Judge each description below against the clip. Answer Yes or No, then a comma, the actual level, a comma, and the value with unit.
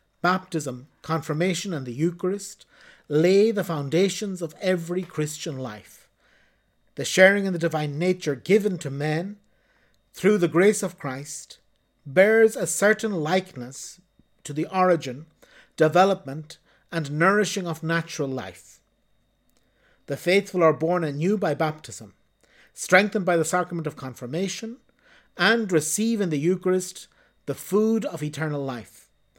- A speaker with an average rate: No, slow, 125 wpm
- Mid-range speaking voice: Yes, medium, 170 Hz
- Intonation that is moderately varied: Yes, average, 4.2 semitones